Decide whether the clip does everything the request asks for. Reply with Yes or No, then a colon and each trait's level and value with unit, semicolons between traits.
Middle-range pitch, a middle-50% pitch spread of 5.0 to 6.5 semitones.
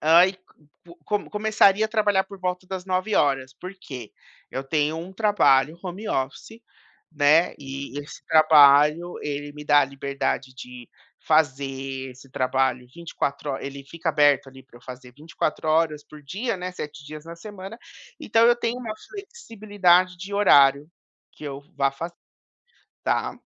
Yes: medium, 155 Hz; wide, 5.4 semitones